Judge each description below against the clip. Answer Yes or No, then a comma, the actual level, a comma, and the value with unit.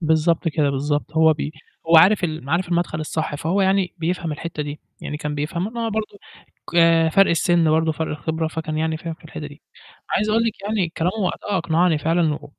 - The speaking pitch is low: No, medium, 160 Hz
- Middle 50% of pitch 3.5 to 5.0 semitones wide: No, narrow, 2.5 semitones